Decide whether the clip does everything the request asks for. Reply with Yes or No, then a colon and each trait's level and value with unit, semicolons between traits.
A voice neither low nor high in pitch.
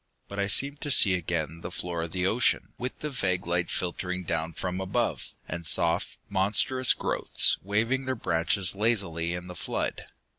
No: very low, 90 Hz